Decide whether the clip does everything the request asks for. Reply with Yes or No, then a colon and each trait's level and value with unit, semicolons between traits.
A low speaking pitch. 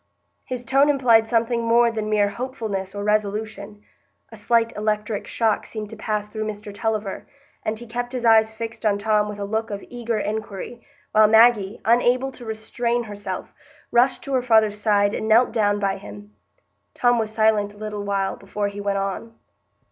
No: high, 220 Hz